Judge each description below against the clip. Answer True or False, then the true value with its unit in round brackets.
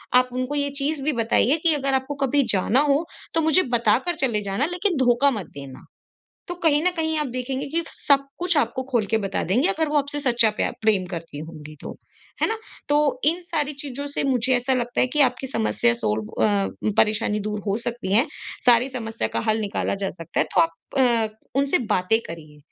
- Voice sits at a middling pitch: False (255 Hz)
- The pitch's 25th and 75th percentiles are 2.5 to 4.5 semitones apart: False (5.1 semitones)